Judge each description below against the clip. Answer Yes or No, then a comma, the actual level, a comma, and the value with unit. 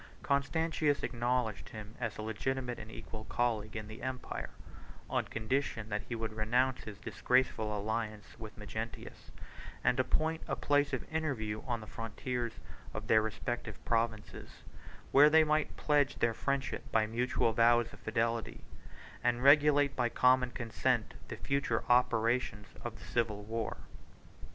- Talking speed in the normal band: Yes, average, 145 wpm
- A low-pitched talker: Yes, low, 120 Hz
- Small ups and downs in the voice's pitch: No, average, 3.1 semitones